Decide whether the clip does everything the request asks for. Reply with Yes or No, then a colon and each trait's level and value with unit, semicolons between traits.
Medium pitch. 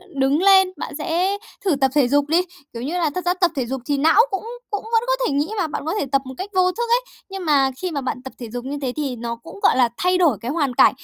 No: very high, 300 Hz